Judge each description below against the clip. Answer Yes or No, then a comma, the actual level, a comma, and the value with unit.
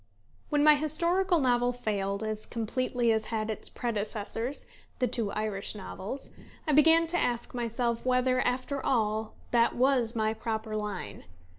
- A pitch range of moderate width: Yes, average, 3.2 semitones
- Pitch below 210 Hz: No, high, 235 Hz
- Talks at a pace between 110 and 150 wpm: Yes, average, 145 wpm